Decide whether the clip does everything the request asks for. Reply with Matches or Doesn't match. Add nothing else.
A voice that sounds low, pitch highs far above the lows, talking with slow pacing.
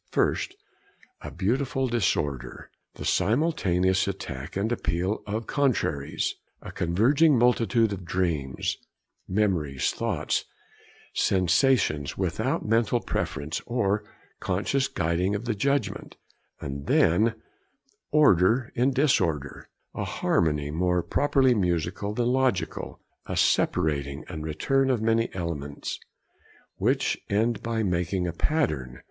Matches